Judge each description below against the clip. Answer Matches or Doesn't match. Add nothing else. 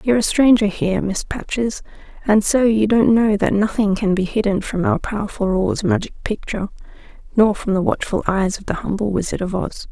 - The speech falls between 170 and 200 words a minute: Matches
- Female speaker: Matches